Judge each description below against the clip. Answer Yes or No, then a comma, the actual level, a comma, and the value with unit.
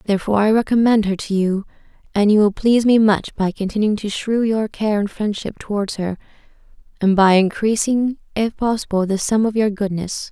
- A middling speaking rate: Yes, average, 185 wpm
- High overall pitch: Yes, high, 210 Hz